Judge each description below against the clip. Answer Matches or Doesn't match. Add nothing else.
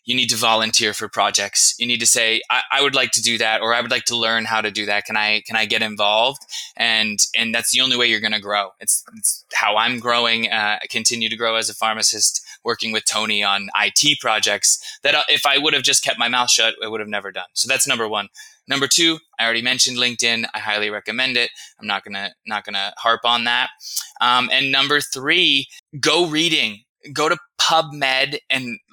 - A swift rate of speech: Matches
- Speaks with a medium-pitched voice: Doesn't match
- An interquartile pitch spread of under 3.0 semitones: Doesn't match